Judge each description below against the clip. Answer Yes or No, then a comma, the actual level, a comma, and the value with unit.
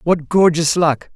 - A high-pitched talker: No, medium, 165 Hz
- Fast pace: No, average, 155 wpm